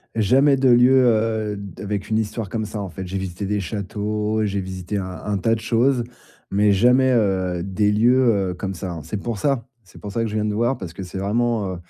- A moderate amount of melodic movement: Yes, average, 3.0 semitones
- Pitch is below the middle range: Yes, low, 105 Hz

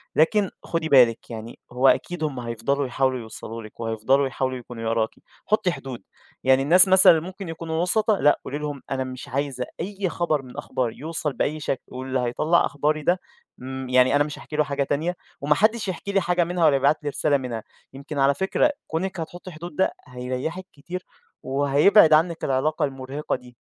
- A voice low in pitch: No, medium, 145 Hz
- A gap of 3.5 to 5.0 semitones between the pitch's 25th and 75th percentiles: Yes, average, 4.5 semitones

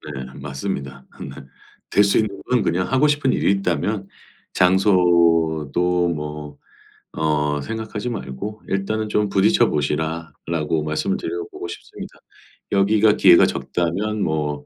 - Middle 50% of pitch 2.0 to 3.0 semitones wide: No, average, 5.3 semitones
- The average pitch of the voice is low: Yes, very low, 90 Hz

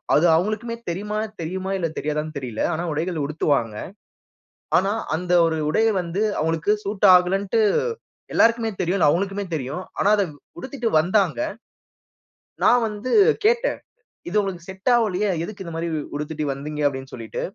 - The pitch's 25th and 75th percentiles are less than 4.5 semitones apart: No, average, 5.1 semitones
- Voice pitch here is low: No, medium, 180 Hz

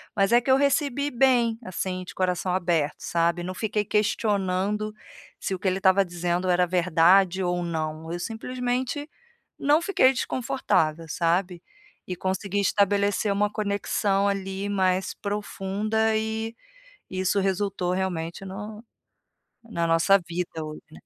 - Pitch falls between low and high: No, high, 195 Hz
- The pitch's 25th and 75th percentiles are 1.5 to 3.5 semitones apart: Yes, average, 3.2 semitones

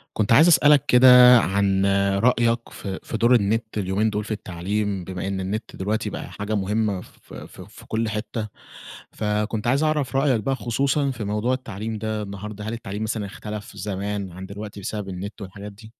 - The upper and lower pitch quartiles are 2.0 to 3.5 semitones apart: Yes, average, 2.7 semitones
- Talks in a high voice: No, low, 105 Hz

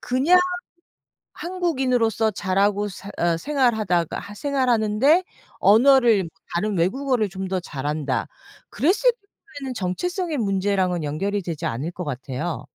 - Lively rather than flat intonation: Yes, wide, 6.8 semitones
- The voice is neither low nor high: No, high, 205 Hz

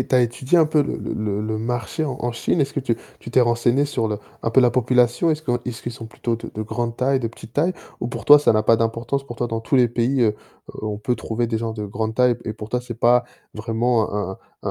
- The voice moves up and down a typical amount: No, narrow, 2.2 semitones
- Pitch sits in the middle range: No, low, 120 Hz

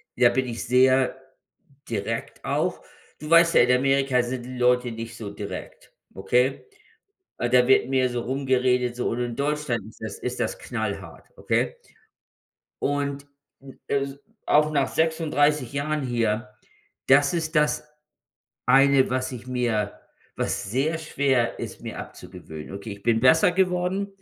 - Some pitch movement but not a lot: Yes, average, 3.2 semitones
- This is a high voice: No, low, 130 Hz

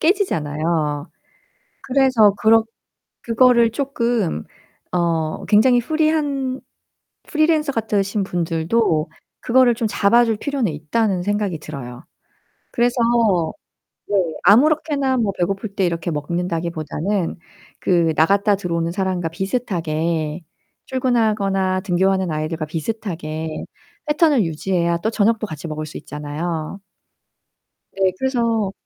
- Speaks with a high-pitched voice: Yes, high, 195 Hz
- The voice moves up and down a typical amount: No, wide, 6.0 semitones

